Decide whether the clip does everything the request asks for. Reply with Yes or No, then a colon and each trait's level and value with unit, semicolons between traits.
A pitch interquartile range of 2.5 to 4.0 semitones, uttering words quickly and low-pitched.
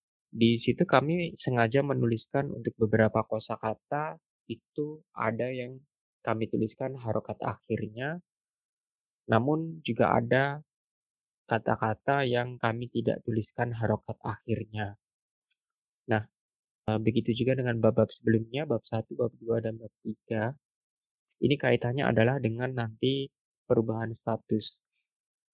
No: average, 3.0 semitones; average, 110 wpm; low, 115 Hz